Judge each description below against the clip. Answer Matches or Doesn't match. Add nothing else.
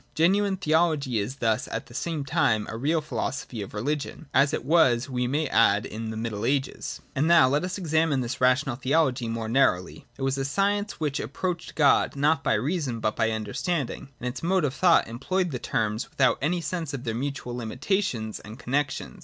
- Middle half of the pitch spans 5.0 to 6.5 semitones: Matches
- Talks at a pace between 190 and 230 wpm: Matches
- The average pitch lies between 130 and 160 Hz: Matches